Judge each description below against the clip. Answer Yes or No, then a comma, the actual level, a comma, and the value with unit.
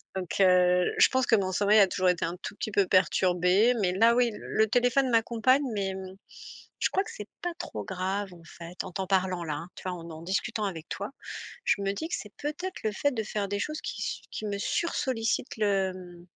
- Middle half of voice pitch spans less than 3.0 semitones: No, average, 3.8 semitones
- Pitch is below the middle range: No, high, 200 Hz